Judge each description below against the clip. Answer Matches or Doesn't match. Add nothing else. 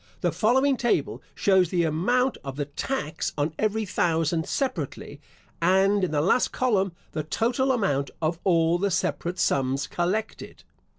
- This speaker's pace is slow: Doesn't match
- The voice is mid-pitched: Matches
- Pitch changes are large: Matches